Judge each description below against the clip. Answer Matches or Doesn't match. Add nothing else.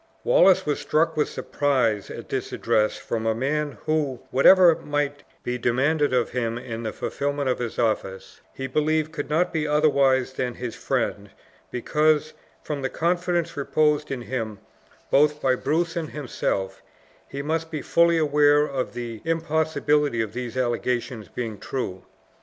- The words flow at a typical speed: Matches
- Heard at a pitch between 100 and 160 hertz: Matches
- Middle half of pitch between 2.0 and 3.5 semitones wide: Doesn't match